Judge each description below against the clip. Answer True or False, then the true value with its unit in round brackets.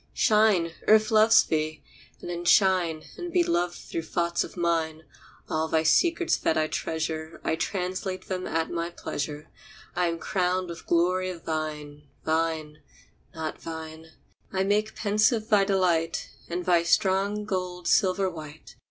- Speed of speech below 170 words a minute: True (150 wpm)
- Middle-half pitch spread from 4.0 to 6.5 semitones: False (3.1 semitones)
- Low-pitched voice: False (175 Hz)